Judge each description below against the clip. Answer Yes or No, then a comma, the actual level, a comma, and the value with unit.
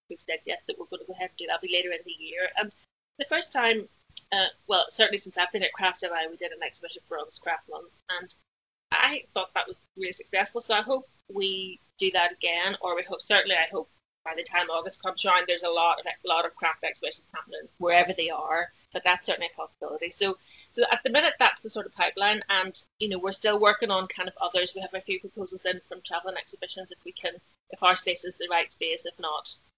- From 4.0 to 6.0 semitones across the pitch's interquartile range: No, average, 2.8 semitones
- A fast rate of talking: Yes, fast, 245 wpm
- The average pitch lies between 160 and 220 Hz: Yes, medium, 185 Hz